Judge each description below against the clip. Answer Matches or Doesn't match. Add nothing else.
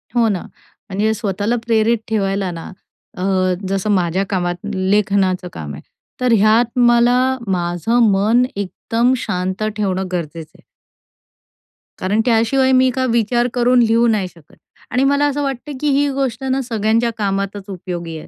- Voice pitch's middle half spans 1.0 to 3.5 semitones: Doesn't match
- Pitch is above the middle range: Matches